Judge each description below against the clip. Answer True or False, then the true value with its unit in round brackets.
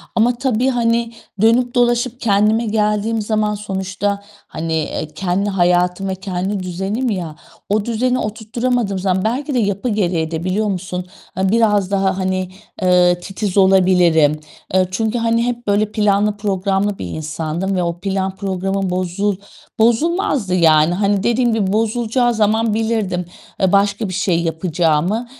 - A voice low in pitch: False (200 Hz)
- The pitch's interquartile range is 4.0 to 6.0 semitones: False (3.3 semitones)